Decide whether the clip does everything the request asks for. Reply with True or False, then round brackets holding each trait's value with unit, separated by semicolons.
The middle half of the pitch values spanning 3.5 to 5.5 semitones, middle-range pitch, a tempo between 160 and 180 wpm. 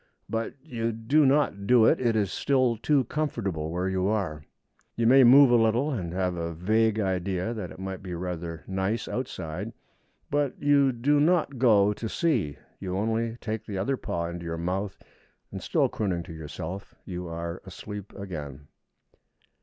False (4.9 semitones; 100 Hz; 170 wpm)